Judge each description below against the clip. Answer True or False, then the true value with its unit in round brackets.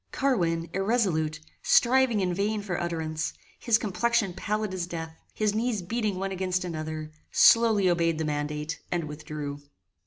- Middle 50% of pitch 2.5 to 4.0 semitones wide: False (5.1 semitones)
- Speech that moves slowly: False (145 wpm)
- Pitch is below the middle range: False (180 Hz)